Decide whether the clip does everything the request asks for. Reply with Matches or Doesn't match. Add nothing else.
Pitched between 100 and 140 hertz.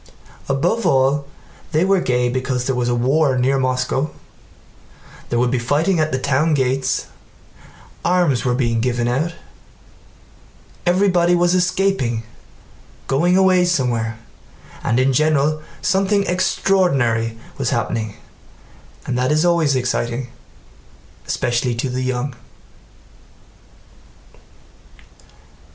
Matches